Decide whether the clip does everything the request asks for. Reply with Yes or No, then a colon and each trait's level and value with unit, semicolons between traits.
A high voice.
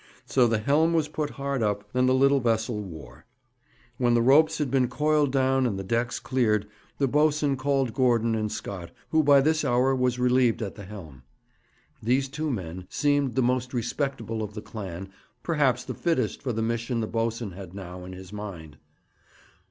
No: low, 125 Hz